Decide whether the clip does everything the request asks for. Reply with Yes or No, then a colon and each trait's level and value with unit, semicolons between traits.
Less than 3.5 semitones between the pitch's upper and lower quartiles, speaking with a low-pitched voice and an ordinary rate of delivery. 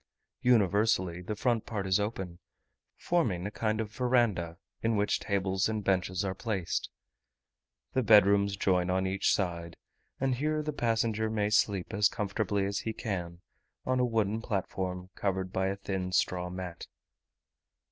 Yes: average, 3.0 semitones; low, 100 Hz; average, 155 wpm